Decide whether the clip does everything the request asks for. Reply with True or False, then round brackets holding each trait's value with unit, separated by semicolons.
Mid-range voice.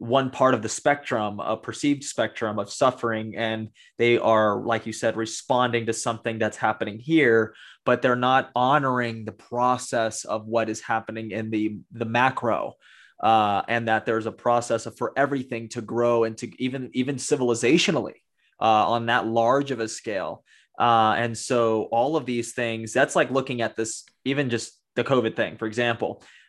False (115 Hz)